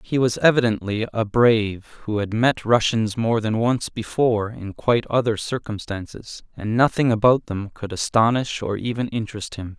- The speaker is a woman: No, male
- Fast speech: No, average, 165 wpm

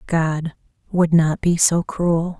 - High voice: No, medium, 165 Hz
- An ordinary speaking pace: Yes, average, 150 wpm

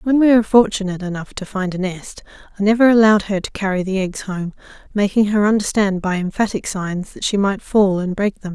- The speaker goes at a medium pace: No, fast, 220 wpm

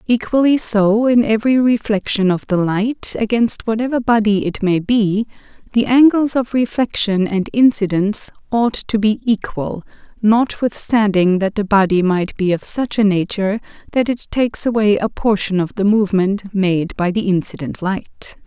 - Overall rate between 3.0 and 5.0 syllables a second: Yes, 4.7 syllables/s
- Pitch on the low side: No, high, 210 Hz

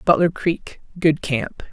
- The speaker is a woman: Yes, female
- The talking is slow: Yes, slow, 105 wpm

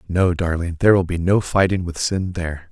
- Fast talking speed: Yes, fast, 220 wpm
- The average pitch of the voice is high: No, very low, 90 Hz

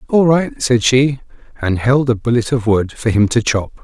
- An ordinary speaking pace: No, fast, 220 wpm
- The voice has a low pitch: Yes, low, 120 Hz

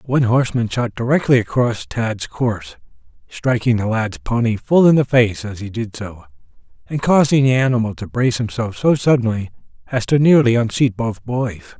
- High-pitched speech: No, low, 115 Hz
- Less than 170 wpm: No, average, 175 wpm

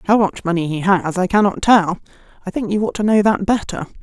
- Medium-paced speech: No, fast, 240 wpm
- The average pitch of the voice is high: Yes, high, 195 Hz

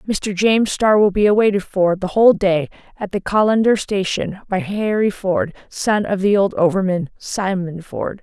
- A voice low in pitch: No, high, 195 Hz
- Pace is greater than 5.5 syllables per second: No, 4.7 syllables/s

